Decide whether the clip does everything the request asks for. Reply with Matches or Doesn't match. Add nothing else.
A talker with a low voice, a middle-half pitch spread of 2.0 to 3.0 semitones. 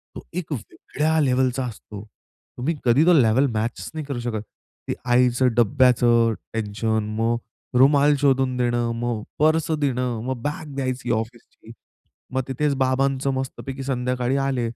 Matches